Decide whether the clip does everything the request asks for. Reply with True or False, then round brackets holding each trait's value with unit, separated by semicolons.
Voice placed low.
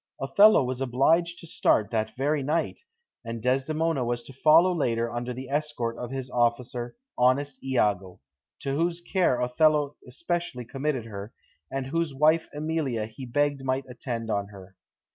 True (130 Hz)